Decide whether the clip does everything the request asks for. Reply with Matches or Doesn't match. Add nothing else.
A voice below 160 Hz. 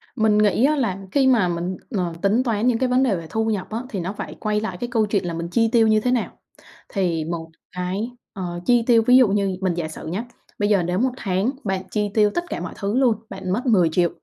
Doesn't match